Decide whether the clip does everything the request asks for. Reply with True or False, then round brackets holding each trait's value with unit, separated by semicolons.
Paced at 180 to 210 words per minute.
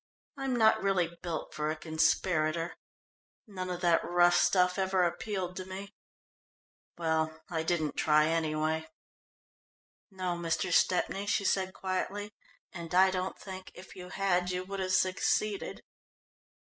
False (135 wpm)